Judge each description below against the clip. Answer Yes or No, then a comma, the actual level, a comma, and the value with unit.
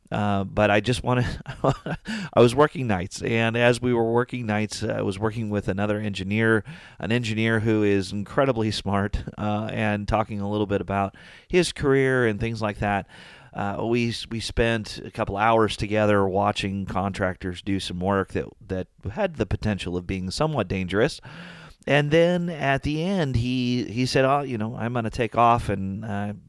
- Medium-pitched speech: No, low, 110 Hz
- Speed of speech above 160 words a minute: Yes, average, 185 wpm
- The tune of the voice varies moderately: Yes, average, 3.2 semitones